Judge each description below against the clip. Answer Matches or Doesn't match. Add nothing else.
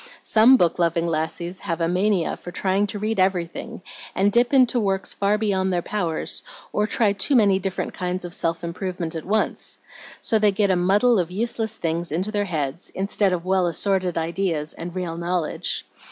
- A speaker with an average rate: Matches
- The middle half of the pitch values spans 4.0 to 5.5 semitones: Doesn't match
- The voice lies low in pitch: Doesn't match